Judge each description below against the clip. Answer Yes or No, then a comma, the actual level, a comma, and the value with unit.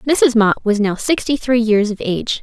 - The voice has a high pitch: Yes, high, 230 Hz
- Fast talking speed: Yes, fast, 225 wpm